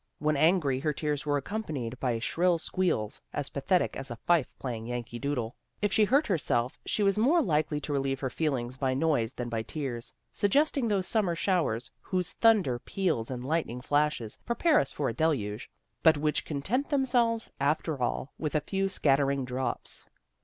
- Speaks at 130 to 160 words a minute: No, average, 175 wpm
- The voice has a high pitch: No, medium, 150 Hz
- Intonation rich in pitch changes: Yes, wide, 6.6 semitones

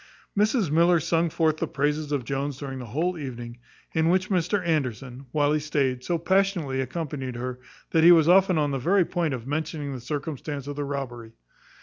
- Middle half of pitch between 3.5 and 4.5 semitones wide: Yes, average, 4.1 semitones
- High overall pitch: No, medium, 150 Hz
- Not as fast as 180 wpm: No, average, 195 wpm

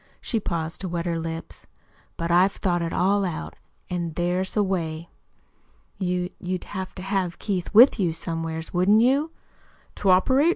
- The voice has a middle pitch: Yes, medium, 180 Hz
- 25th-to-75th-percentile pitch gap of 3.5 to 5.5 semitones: No, narrow, 2.6 semitones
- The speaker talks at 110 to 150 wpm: No, average, 165 wpm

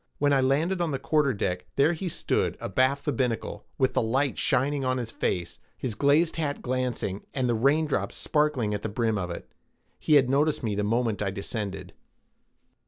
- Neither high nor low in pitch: No, low, 130 Hz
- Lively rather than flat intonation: No, average, 4.8 semitones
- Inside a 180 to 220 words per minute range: Yes, average, 185 wpm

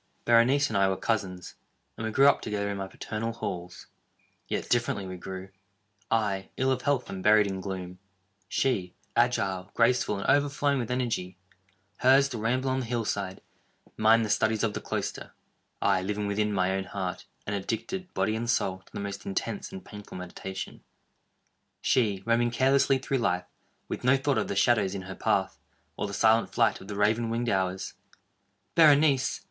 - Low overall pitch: Yes, low, 105 Hz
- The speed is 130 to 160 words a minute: No, average, 170 wpm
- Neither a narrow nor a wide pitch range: Yes, average, 4.1 semitones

